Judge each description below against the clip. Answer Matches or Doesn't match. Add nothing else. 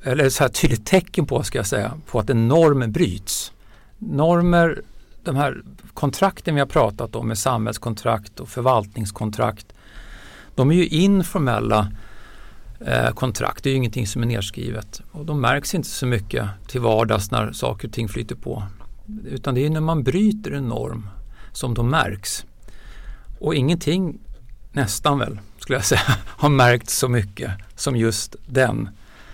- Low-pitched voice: Matches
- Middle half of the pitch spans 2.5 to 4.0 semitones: Doesn't match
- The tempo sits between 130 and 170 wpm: Matches